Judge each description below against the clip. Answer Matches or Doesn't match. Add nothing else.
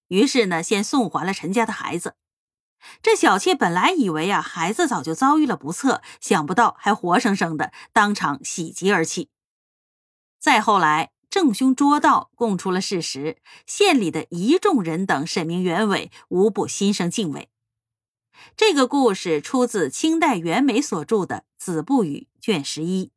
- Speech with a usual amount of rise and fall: Doesn't match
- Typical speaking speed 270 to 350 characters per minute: Doesn't match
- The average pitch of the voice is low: Doesn't match